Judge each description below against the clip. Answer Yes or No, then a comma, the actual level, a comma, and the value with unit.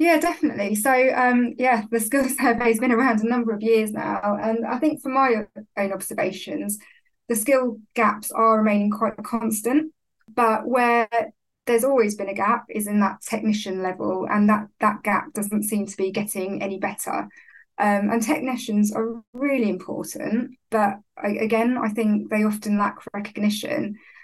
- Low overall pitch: No, high, 225 Hz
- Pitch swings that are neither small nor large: Yes, average, 3.0 semitones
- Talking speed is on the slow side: No, average, 165 wpm